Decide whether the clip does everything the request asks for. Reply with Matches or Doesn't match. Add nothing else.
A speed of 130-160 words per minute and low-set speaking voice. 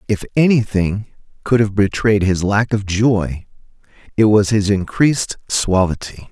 Matches